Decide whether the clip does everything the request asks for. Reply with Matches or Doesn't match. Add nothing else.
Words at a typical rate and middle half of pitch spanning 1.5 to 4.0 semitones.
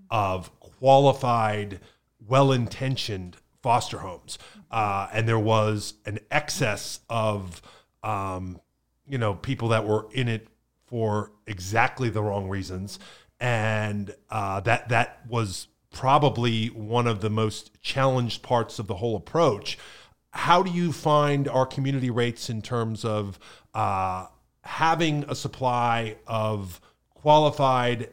Doesn't match